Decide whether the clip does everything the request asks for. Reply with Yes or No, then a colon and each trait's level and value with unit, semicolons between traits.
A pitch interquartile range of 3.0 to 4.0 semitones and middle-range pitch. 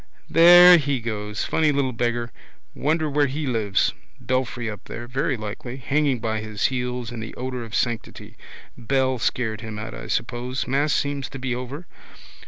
No: average, 3.4 semitones; low, 125 Hz